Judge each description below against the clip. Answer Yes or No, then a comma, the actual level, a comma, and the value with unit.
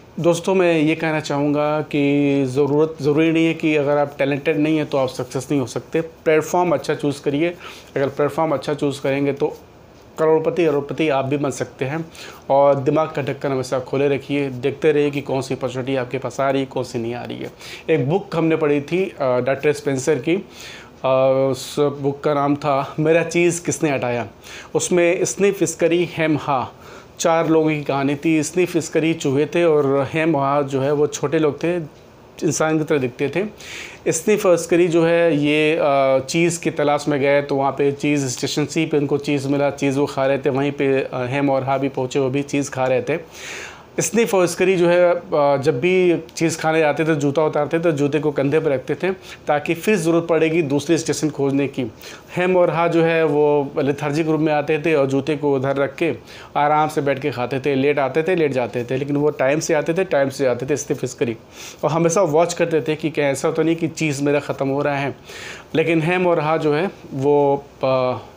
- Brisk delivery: Yes, fast, 210 wpm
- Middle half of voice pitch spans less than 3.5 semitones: Yes, average, 2.7 semitones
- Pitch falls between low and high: Yes, medium, 150 Hz